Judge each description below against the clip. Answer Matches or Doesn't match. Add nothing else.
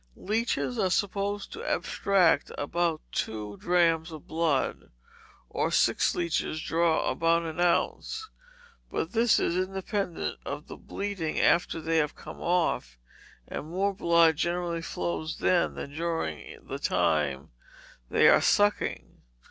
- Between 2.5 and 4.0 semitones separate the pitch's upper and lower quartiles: Matches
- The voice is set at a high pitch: Doesn't match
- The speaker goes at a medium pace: Doesn't match